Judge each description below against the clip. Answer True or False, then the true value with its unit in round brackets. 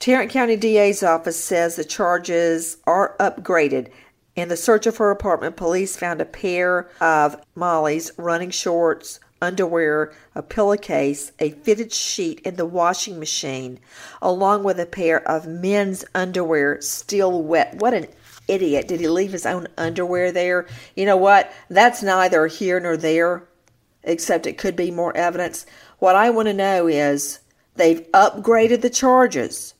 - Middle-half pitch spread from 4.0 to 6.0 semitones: False (3.0 semitones)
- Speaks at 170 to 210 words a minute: False (155 wpm)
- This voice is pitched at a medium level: True (175 Hz)